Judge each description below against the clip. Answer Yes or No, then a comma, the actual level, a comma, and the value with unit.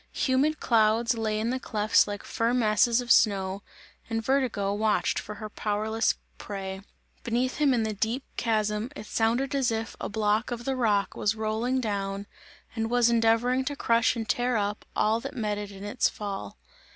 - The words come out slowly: No, average, 180 wpm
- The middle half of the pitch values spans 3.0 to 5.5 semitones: No, narrow, 2.5 semitones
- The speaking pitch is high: Yes, high, 225 Hz